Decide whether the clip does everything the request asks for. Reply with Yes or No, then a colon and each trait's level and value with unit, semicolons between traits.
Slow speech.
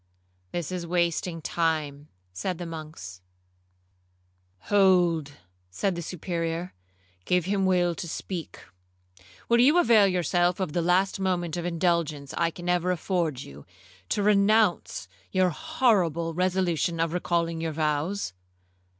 Yes: slow, 125 wpm